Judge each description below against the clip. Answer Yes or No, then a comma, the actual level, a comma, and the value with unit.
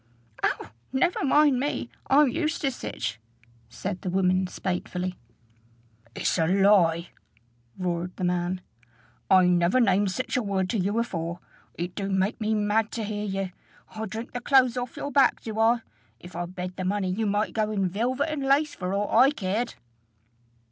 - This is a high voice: Yes, high, 205 Hz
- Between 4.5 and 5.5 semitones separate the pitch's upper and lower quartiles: Yes, average, 4.9 semitones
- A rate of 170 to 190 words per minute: Yes, average, 175 wpm